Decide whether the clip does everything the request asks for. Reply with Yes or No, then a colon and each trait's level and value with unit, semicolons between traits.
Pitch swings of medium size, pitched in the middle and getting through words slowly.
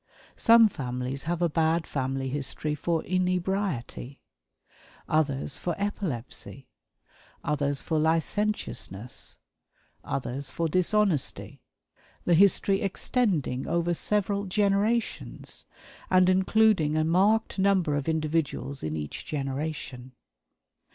No: wide, 5.8 semitones; medium, 160 Hz; slow, 95 wpm